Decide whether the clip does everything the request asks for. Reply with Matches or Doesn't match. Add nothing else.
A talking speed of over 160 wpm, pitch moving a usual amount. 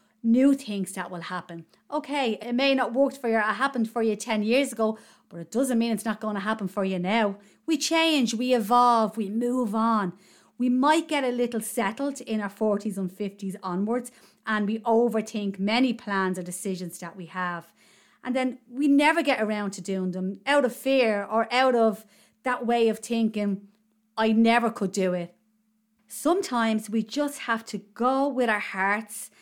Matches